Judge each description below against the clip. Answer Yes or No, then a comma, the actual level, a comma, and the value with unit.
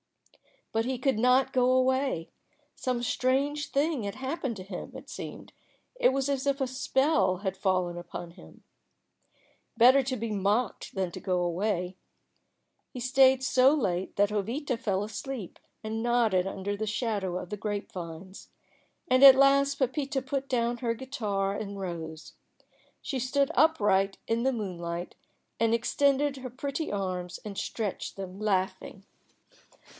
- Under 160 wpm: Yes, average, 150 wpm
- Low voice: No, high, 230 Hz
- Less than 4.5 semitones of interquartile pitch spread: No, wide, 5.5 semitones